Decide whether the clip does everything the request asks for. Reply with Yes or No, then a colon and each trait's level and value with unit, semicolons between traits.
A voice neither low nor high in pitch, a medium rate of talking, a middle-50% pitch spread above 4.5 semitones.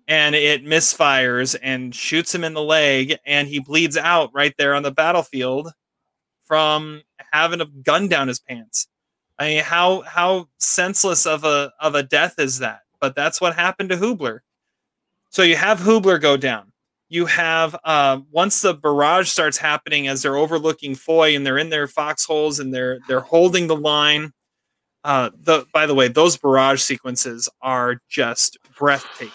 No: medium, 150 Hz; average, 170 wpm; average, 3.2 semitones